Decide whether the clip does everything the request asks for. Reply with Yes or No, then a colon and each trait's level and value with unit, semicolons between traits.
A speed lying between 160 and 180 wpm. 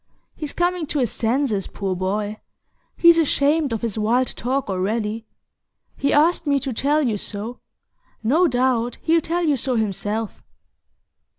No: average, 150 wpm